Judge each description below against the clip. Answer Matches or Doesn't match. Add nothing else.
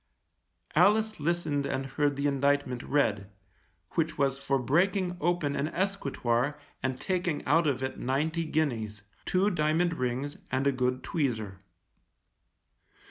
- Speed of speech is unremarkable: Doesn't match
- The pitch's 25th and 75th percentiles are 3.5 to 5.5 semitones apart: Matches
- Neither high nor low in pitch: Matches